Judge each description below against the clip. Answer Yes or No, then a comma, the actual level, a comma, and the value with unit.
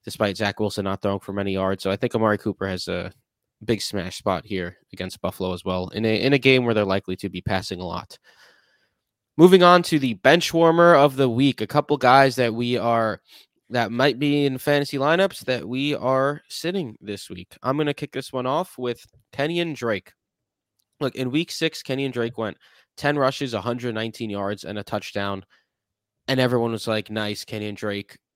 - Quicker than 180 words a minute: Yes, average, 200 wpm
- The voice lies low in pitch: Yes, low, 115 Hz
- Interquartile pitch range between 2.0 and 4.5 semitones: No, average, 5.3 semitones